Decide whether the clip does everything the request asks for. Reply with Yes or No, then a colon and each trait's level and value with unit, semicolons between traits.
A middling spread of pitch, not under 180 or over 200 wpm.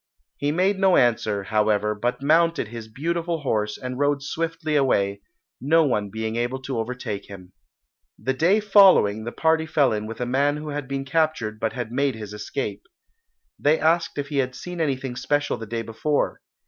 No: wide, 5.9 semitones; average, 185 wpm